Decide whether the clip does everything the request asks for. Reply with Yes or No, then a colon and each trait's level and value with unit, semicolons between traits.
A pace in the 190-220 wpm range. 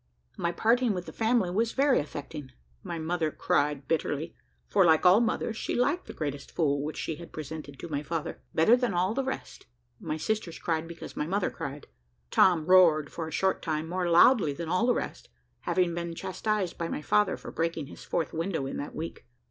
Yes: fast, 205 wpm